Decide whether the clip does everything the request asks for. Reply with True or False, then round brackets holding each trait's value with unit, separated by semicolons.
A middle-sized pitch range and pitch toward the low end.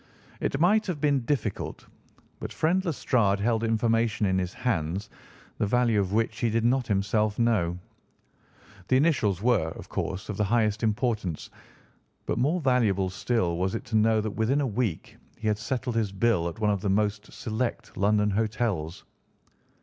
True (3.3 semitones; 110 Hz)